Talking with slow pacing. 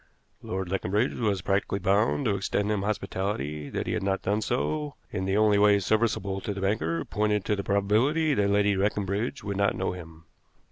No: average, 190 wpm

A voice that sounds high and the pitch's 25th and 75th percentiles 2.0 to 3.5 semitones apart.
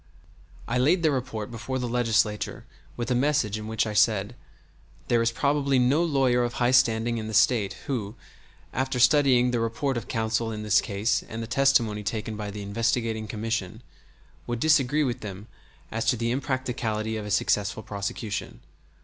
No: low, 115 Hz; average, 2.9 semitones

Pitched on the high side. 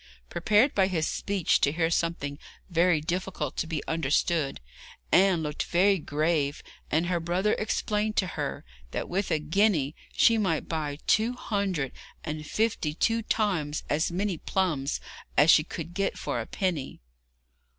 No: medium, 170 Hz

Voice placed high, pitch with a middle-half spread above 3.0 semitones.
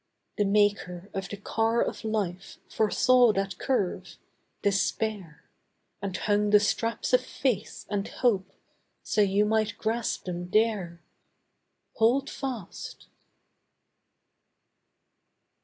No: high, 210 Hz; narrow, 2.6 semitones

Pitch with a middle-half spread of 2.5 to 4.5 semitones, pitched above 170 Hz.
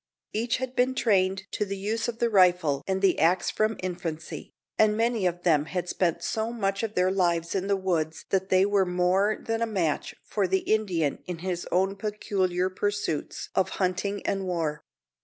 Yes: average, 2.8 semitones; high, 190 Hz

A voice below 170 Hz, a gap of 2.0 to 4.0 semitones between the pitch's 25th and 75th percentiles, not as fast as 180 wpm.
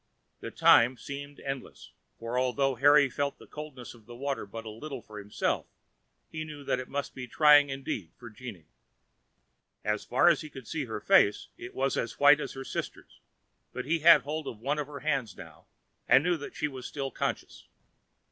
No: low, 135 Hz; average, 3.6 semitones; average, 195 wpm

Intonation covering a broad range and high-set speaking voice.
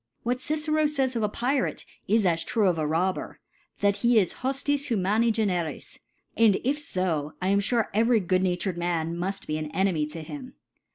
Yes: wide, 5.7 semitones; high, 200 Hz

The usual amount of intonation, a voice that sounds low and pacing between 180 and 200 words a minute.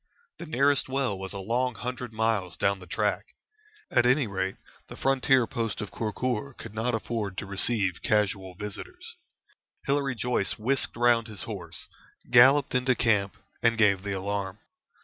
No: average, 4.2 semitones; low, 110 Hz; average, 155 wpm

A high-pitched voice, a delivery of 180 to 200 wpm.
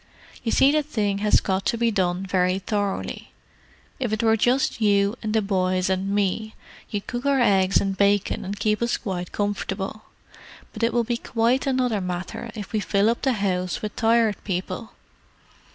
Yes: high, 205 Hz; average, 185 wpm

